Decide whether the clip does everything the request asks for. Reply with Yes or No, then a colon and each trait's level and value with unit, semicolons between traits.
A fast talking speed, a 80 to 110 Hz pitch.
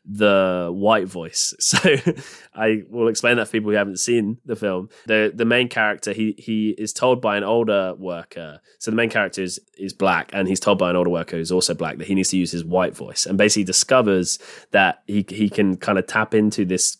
Yes: fast, 230 wpm; low, 100 Hz